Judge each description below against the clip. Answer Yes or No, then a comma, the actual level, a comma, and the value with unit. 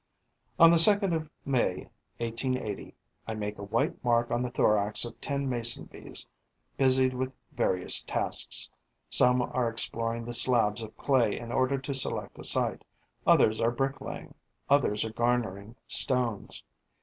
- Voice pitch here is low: Yes, low, 120 Hz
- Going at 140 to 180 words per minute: Yes, average, 150 wpm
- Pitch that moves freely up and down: No, narrow, 2.6 semitones